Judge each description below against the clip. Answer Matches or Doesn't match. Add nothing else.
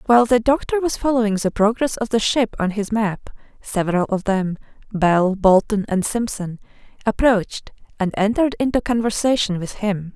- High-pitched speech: Matches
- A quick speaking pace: Doesn't match